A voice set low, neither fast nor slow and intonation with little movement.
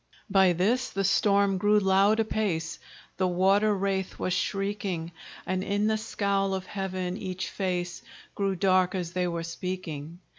No: high, 190 Hz; average, 150 wpm; narrow, 1.8 semitones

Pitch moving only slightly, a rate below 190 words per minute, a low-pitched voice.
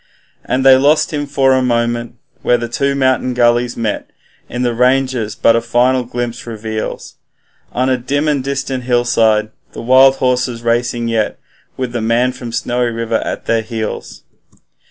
Yes: narrow, 1.9 semitones; average, 160 wpm; low, 120 Hz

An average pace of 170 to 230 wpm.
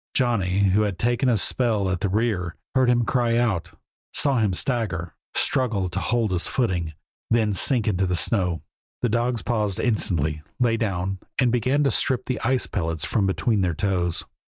Yes: average, 180 wpm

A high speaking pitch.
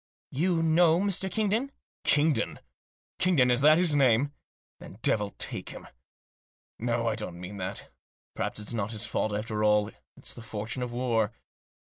No: low, 120 Hz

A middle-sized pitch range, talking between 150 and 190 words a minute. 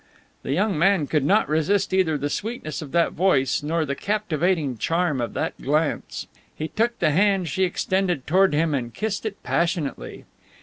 Yes: average, 4.7 semitones; average, 175 wpm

